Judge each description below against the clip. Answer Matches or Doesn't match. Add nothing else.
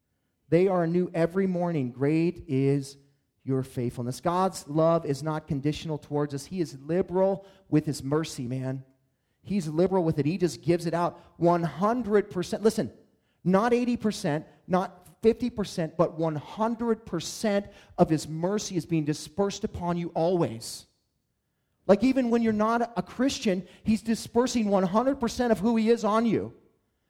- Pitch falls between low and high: Matches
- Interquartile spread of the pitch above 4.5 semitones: Matches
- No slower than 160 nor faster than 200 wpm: Doesn't match